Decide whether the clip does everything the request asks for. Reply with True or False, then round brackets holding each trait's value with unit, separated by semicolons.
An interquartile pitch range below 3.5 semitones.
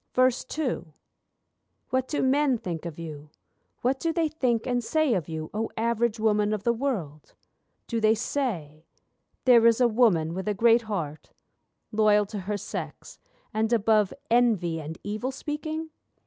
False (5.0 semitones)